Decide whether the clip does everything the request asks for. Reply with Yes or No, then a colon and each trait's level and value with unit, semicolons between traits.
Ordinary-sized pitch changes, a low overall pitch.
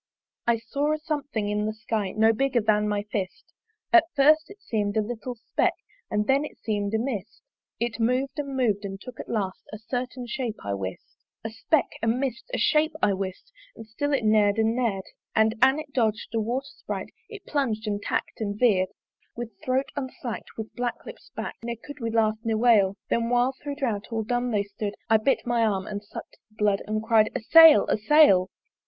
No: average, 3.8 semitones; high, 225 Hz